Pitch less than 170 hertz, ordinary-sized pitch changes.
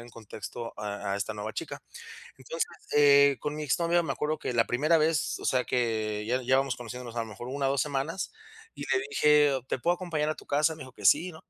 Yes: low, 135 Hz; average, 4.5 semitones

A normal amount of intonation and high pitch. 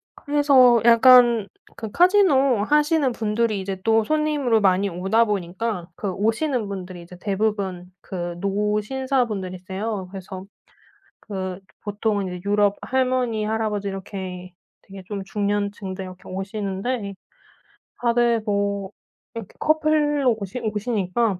Yes: average, 3.8 semitones; high, 210 Hz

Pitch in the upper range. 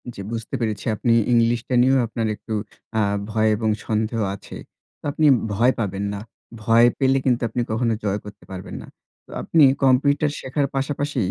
No: low, 115 Hz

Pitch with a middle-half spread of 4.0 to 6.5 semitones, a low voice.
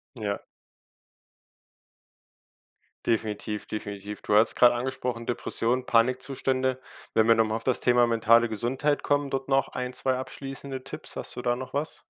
No: narrow, 2.5 semitones; low, 125 Hz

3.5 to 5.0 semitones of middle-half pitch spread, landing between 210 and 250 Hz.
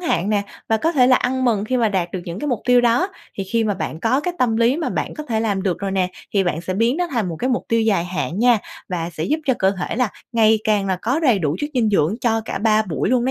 Yes: average, 4.5 semitones; high, 220 Hz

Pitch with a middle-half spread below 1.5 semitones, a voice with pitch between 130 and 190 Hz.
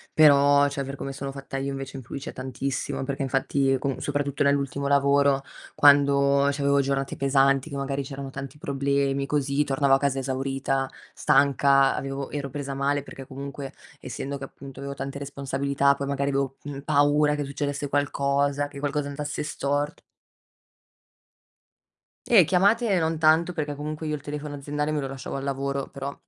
Yes: narrow, 0.8 semitones; medium, 140 Hz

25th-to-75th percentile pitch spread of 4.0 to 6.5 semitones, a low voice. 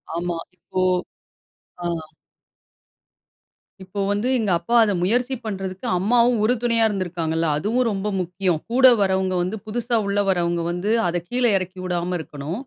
No: average, 4.3 semitones; high, 190 Hz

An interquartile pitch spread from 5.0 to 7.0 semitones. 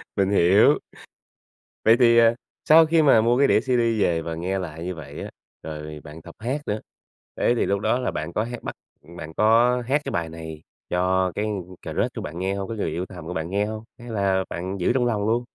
Yes: wide, 5.6 semitones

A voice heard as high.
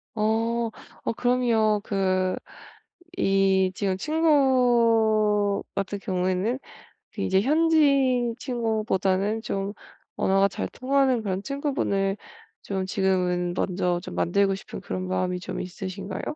Yes: high, 205 Hz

